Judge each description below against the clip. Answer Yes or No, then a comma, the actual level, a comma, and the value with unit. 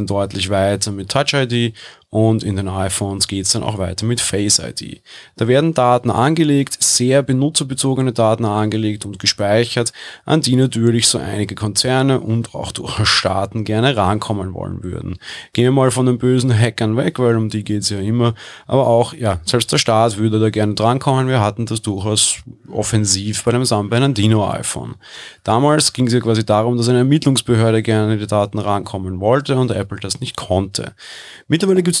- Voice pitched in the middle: No, low, 115 Hz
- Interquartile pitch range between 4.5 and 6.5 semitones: No, average, 3.5 semitones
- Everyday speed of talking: Yes, average, 180 wpm